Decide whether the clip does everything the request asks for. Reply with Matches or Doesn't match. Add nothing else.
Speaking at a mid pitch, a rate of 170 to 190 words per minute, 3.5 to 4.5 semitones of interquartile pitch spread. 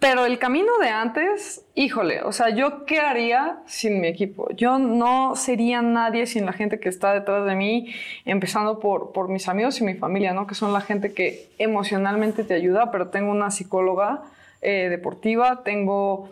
Doesn't match